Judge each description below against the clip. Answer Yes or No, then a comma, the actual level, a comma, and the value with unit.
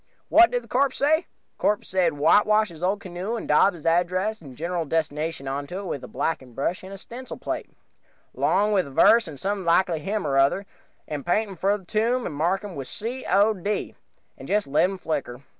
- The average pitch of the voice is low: No, medium, 185 Hz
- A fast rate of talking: Yes, fast, 210 wpm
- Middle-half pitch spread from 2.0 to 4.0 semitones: No, average, 5.1 semitones